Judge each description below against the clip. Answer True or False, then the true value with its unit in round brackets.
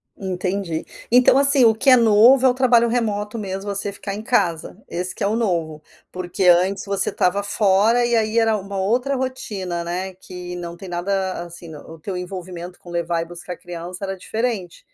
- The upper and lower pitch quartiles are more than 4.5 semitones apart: False (4.1 semitones)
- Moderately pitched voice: False (195 Hz)